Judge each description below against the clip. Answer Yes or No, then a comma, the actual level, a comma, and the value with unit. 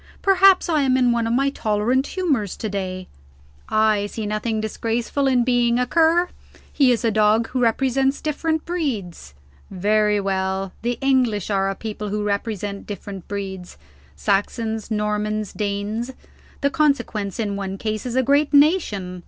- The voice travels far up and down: No, average, 4.4 semitones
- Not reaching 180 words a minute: Yes, average, 155 wpm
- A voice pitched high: Yes, high, 220 Hz